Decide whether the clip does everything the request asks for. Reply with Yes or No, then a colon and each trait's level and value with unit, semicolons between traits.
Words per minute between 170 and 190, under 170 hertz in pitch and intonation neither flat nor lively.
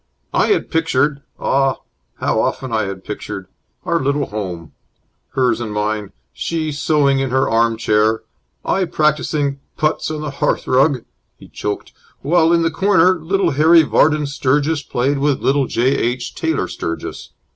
No: average, 155 wpm; medium, 140 Hz; average, 4.8 semitones